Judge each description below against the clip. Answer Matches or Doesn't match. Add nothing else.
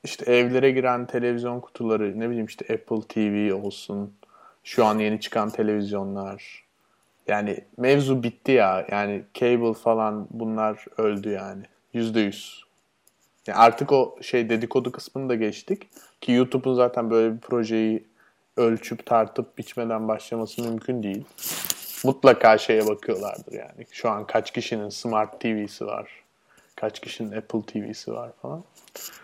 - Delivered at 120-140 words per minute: Matches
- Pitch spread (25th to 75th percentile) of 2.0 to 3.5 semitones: Matches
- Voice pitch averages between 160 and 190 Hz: Doesn't match